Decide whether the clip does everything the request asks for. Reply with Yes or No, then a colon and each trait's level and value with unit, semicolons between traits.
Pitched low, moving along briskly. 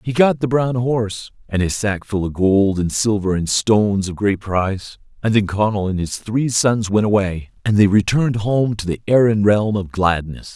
Yes: low, 105 Hz; fast, 210 wpm